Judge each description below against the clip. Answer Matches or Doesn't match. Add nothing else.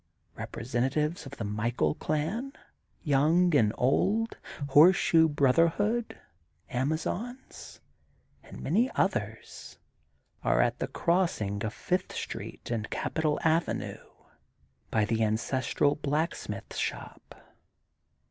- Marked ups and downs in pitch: Matches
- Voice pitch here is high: Doesn't match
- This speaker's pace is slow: Matches